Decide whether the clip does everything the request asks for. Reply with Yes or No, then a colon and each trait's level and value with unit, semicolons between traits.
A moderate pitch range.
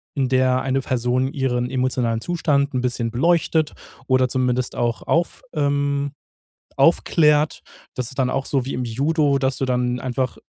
No: narrow, 2.1 semitones